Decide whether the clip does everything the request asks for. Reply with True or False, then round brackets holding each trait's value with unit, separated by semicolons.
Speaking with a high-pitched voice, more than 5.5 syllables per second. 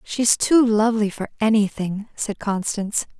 False (215 Hz; 4.6 syllables/s)